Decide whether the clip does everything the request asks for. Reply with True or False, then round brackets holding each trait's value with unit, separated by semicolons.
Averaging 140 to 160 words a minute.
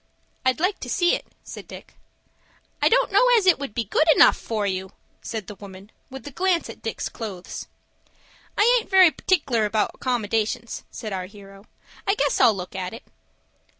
False (185 wpm)